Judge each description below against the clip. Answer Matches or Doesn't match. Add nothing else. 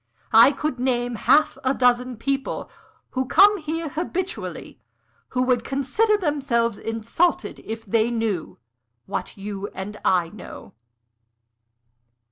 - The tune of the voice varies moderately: Matches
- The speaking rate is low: Matches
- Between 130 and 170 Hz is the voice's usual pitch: Doesn't match